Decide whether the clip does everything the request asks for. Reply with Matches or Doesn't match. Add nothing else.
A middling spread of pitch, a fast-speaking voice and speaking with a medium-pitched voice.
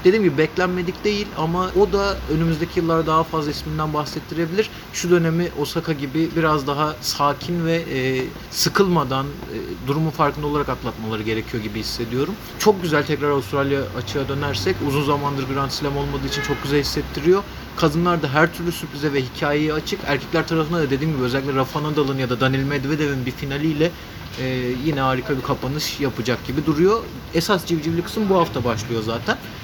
Matches